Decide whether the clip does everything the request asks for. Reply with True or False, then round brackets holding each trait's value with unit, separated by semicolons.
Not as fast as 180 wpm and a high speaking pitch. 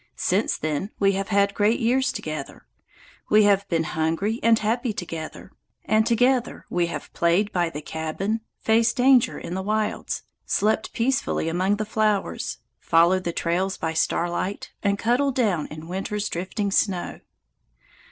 True (150 wpm; 200 Hz)